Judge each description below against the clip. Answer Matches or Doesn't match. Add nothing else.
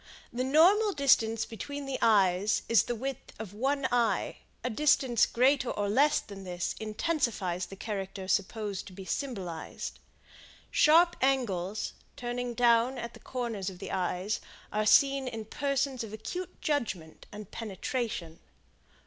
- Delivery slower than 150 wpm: Matches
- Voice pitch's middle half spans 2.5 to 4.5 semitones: Doesn't match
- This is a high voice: Matches